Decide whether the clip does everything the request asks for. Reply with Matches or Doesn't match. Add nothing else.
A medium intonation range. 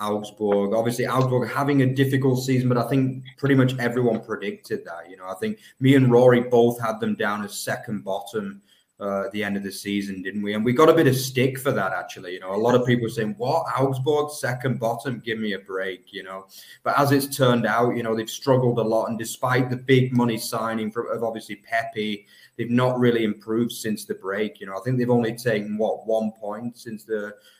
Matches